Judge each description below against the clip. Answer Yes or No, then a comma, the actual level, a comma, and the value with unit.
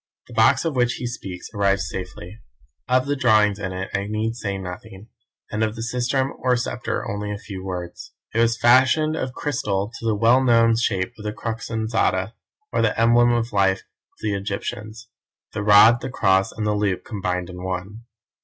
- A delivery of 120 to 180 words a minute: No, average, 190 wpm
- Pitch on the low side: Yes, low, 110 Hz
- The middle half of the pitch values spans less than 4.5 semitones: Yes, average, 3.4 semitones